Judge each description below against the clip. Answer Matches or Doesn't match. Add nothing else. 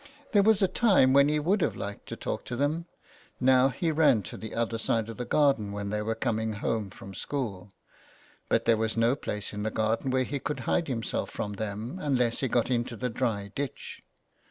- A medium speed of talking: Doesn't match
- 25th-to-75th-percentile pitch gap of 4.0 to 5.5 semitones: Matches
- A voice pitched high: Doesn't match